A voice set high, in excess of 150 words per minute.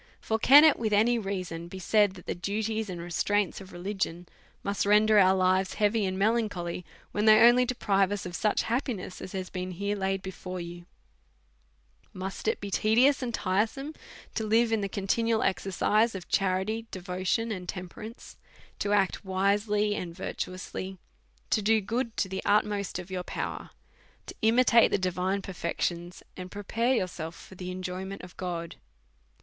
Yes: high, 195 Hz; average, 170 wpm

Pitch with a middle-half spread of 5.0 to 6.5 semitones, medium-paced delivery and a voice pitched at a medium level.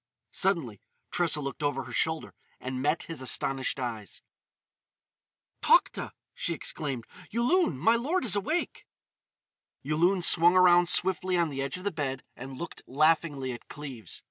Yes: wide, 5.4 semitones; average, 145 wpm; medium, 155 Hz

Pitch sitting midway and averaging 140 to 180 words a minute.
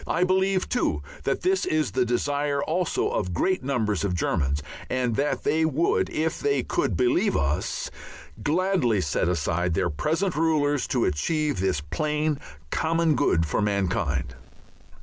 Yes: medium, 145 Hz; average, 150 wpm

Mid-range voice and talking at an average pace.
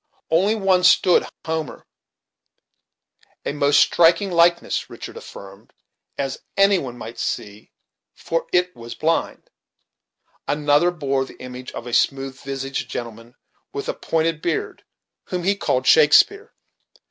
No: medium, 150 Hz; slow, 125 wpm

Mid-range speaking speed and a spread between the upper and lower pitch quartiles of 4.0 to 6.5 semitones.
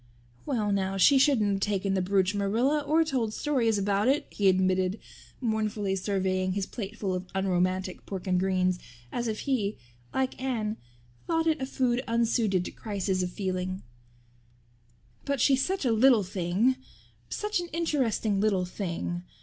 Yes: average, 155 wpm; average, 5.3 semitones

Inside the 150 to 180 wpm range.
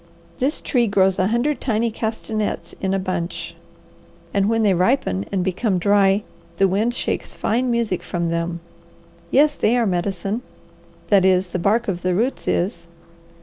Yes: average, 160 wpm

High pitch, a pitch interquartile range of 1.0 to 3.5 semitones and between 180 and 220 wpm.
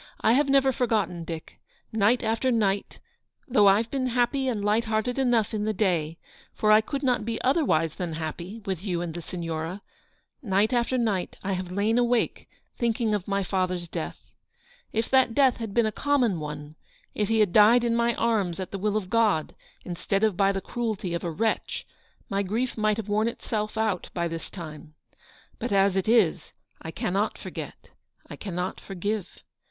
No: high, 210 Hz; average, 4.2 semitones; average, 190 wpm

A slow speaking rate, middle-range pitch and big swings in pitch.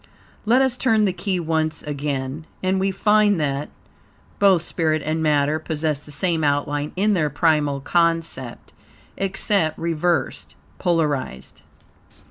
No: slow, 125 wpm; medium, 160 Hz; average, 4.1 semitones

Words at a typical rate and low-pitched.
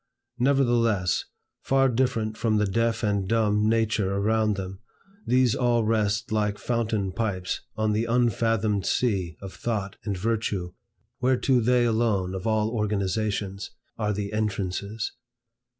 No: slow, 130 wpm; low, 110 Hz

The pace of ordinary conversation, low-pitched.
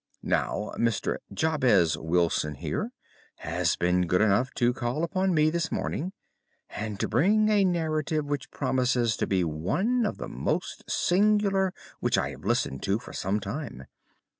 Yes: average, 155 wpm; low, 125 Hz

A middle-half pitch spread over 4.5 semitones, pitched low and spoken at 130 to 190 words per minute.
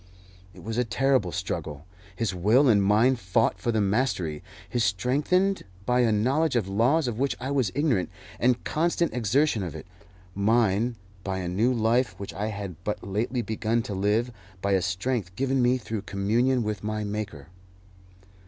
No: average, 4.2 semitones; low, 110 Hz; average, 170 wpm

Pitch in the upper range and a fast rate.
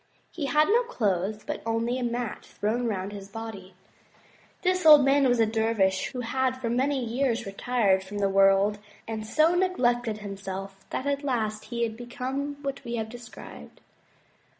No: high, 235 Hz; average, 170 wpm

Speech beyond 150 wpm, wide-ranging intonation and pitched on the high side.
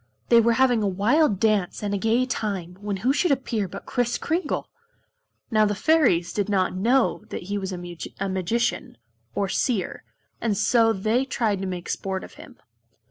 No: average, 180 wpm; average, 3.8 semitones; high, 210 Hz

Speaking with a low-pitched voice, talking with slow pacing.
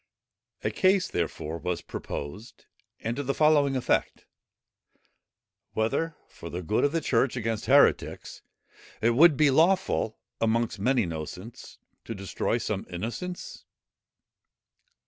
Yes: low, 115 Hz; slow, 120 wpm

